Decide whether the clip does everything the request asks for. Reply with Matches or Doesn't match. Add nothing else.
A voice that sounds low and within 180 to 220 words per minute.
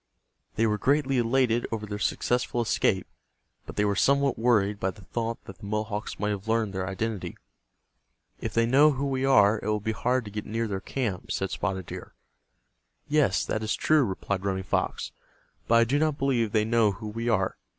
Matches